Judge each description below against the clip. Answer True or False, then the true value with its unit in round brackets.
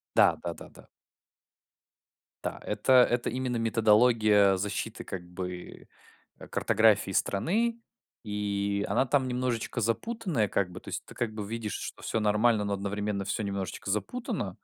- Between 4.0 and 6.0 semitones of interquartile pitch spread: False (3.2 semitones)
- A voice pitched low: True (105 Hz)